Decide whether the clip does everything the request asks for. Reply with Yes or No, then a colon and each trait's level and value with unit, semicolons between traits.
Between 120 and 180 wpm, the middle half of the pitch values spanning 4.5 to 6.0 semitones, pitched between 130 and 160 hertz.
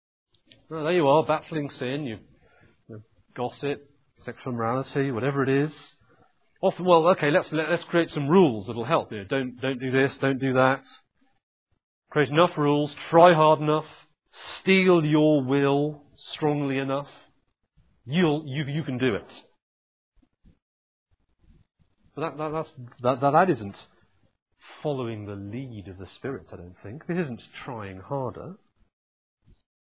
Yes: average, 145 wpm; wide, 5.4 semitones; low, 135 Hz